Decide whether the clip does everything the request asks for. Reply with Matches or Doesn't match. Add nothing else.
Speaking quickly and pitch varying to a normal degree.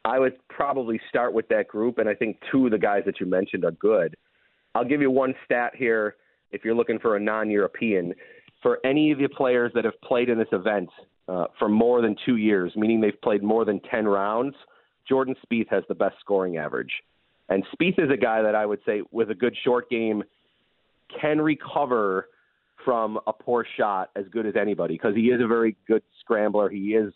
Matches